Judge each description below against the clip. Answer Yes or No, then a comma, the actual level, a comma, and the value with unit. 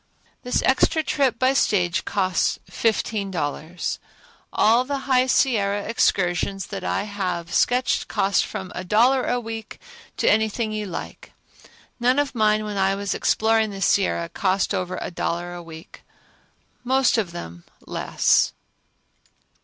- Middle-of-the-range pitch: No, high, 205 Hz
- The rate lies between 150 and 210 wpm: No, average, 140 wpm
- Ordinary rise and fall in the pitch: Yes, average, 4.6 semitones